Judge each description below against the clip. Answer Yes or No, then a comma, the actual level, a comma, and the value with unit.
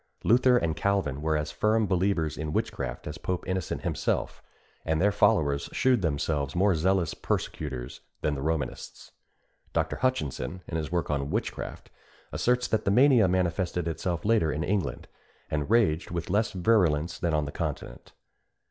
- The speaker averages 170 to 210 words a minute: No, average, 155 wpm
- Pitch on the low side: Yes, very low, 85 Hz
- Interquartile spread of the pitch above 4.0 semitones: Yes, average, 4.7 semitones